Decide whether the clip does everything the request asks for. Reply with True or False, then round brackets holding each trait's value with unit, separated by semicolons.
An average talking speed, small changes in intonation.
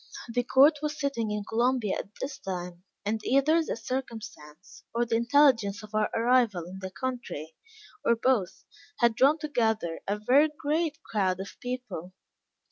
False (155 wpm; 4.8 semitones)